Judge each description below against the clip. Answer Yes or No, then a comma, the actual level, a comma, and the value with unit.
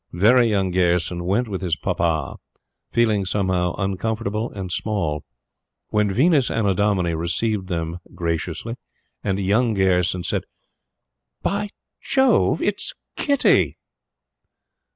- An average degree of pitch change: Yes, average, 4.0 semitones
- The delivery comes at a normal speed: No, slow, 105 wpm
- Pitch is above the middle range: No, very low, 95 Hz